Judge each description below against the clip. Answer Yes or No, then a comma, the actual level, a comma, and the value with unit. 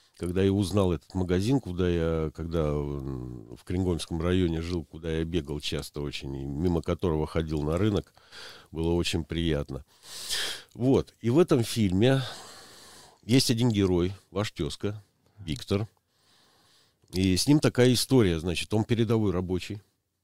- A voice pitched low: Yes, very low, 90 Hz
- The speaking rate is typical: Yes, average, 135 wpm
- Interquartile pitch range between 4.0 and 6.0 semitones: Yes, average, 4.4 semitones